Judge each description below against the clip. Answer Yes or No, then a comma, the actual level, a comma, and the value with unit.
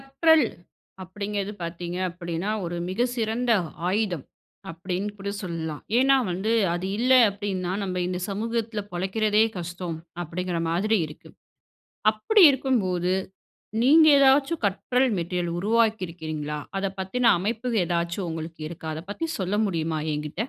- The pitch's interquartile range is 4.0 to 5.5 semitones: Yes, average, 4.7 semitones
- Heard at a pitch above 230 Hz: No, high, 190 Hz